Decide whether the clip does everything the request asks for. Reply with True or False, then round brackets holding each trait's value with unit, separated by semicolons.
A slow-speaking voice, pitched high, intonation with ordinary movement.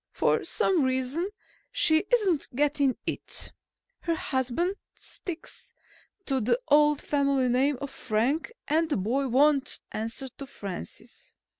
True (125 wpm; 280 Hz; 3.5 semitones)